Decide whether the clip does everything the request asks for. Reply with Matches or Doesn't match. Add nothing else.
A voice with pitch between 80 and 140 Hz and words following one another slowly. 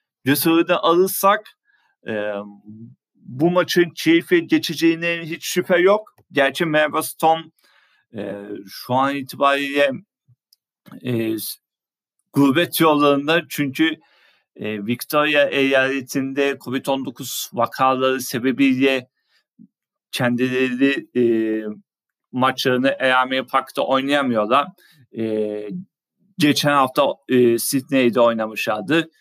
Matches